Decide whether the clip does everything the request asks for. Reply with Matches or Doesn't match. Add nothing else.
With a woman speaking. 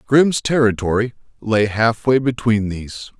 Doesn't match